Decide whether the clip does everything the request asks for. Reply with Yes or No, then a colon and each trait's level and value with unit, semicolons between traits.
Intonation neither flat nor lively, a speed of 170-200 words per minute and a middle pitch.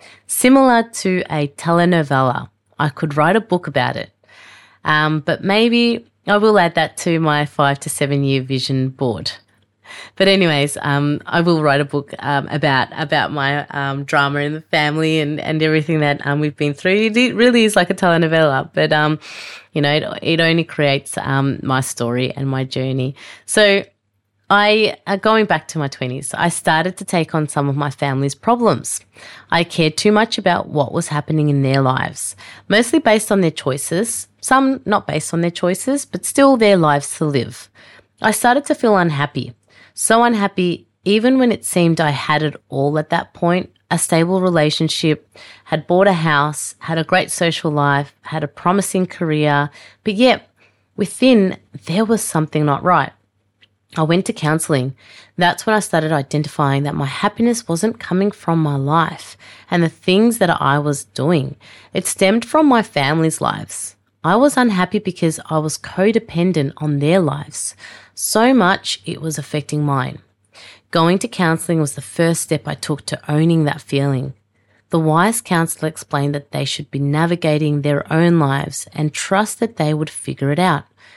Yes: average, 4.4 semitones; average, 175 wpm; medium, 155 Hz